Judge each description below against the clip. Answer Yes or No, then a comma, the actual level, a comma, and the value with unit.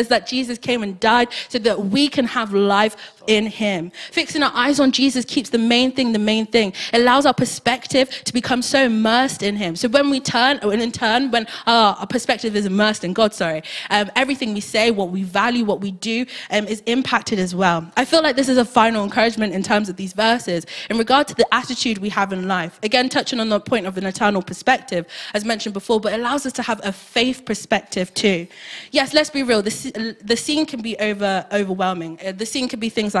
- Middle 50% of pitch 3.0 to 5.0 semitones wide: Yes, average, 3.7 semitones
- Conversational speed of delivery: No, fast, 230 wpm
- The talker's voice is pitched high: Yes, high, 225 Hz